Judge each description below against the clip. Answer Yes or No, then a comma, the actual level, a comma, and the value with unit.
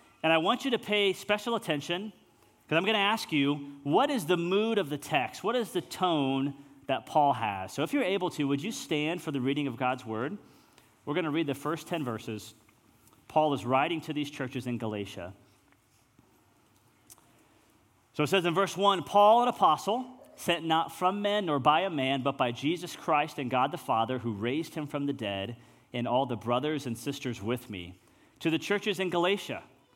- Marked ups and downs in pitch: Yes, wide, 6.5 semitones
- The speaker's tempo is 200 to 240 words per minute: Yes, fast, 205 wpm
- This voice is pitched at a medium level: Yes, medium, 145 Hz